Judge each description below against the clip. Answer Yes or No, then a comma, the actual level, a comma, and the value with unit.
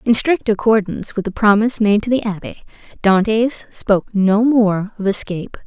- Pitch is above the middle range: Yes, high, 210 Hz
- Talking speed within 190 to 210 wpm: No, average, 170 wpm